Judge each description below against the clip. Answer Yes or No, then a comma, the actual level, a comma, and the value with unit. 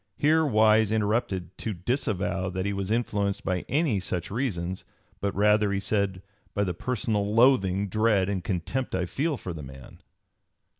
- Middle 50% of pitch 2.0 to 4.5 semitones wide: Yes, average, 3.0 semitones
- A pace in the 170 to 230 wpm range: No, average, 160 wpm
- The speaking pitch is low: Yes, low, 100 Hz